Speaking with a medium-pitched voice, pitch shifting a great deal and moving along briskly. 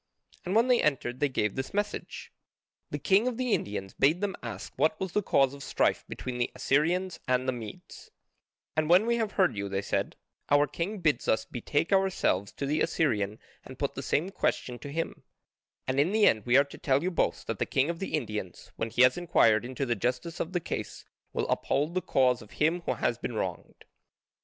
Yes: medium, 145 Hz; wide, 6.4 semitones; fast, 215 wpm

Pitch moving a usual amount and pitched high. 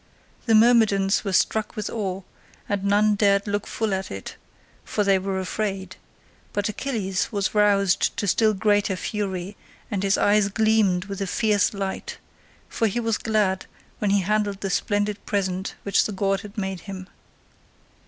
No: narrow, 1.6 semitones; high, 200 Hz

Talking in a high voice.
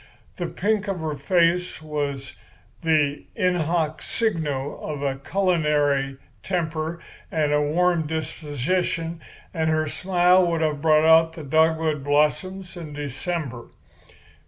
No: medium, 160 Hz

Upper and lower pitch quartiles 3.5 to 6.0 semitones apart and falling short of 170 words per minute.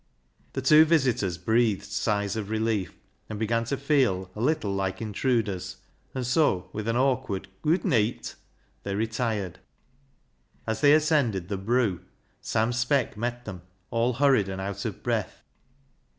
Yes: average, 4.3 semitones; average, 150 wpm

